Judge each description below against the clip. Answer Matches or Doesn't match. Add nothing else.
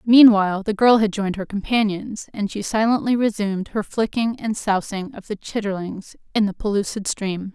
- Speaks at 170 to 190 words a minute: Matches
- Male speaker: Doesn't match